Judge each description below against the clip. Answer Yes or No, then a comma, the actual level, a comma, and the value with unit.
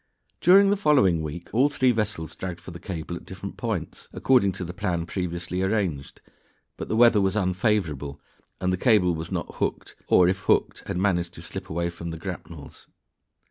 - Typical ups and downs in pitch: Yes, average, 3.7 semitones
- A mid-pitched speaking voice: No, very low, 90 Hz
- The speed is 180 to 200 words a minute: Yes, average, 185 wpm